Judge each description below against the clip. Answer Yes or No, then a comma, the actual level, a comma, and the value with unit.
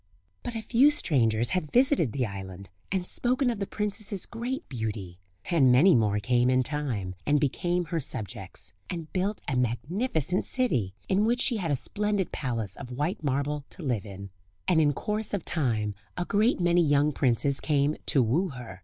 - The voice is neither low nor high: Yes, medium, 150 Hz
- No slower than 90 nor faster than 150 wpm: No, average, 180 wpm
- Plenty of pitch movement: Yes, wide, 8.0 semitones